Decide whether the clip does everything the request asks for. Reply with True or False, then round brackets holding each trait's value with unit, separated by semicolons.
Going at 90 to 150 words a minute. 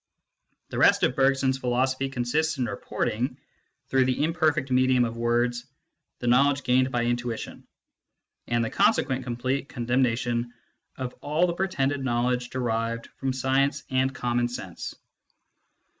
True (140 wpm)